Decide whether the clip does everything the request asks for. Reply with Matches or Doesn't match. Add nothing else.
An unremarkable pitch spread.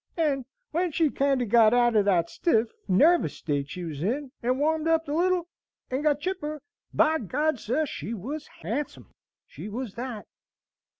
Doesn't match